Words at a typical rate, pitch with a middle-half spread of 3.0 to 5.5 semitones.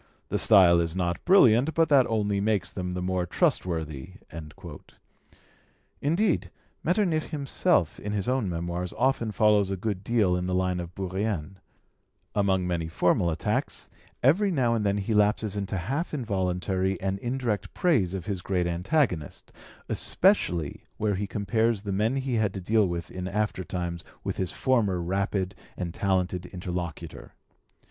Yes: average, 150 wpm; average, 3.9 semitones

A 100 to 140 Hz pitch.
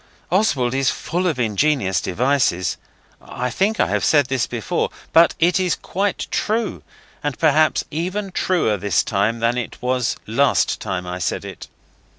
Yes: low, 135 Hz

